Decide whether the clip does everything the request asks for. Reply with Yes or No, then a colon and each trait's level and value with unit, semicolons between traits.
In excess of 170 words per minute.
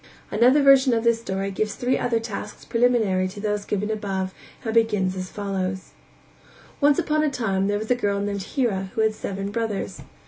Yes: average, 185 wpm